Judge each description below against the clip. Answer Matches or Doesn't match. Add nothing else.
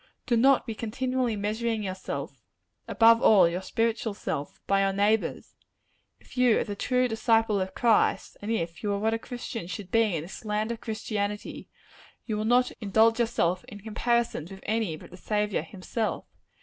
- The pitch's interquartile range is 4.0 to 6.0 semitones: Doesn't match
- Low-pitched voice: Doesn't match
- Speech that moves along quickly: Doesn't match